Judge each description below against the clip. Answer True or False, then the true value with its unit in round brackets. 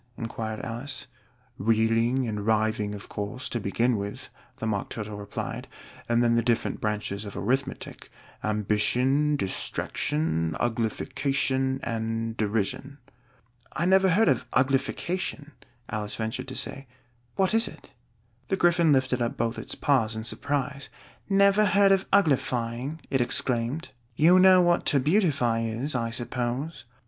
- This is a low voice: True (125 Hz)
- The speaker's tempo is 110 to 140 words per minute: True (135 wpm)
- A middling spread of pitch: True (4.4 semitones)